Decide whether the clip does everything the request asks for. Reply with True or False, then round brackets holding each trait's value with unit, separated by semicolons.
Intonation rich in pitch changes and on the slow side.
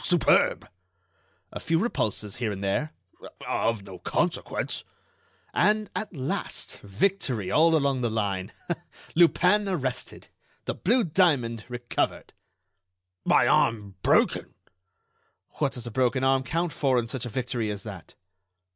True (7.0 semitones; 130 wpm)